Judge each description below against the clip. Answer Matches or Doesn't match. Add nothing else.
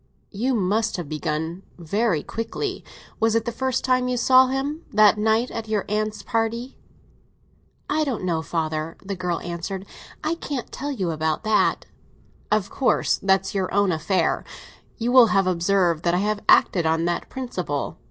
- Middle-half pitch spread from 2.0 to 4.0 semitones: Doesn't match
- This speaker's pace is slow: Doesn't match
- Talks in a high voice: Matches